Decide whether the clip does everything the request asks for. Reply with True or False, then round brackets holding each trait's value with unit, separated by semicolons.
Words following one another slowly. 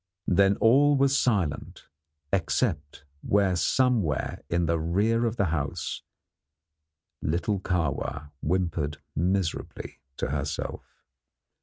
True (100 wpm)